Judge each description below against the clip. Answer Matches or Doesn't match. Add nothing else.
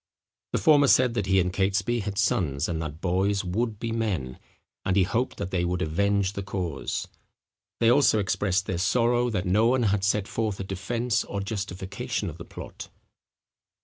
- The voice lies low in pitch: Matches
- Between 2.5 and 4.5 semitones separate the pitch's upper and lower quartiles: Matches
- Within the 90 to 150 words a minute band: Doesn't match